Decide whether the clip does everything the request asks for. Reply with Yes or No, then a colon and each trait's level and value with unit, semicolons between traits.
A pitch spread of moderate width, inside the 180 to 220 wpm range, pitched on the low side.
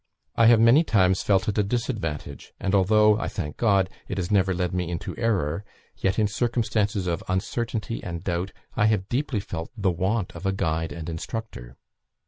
Yes: average, 3.7 semitones; average, 185 wpm; very low, 95 Hz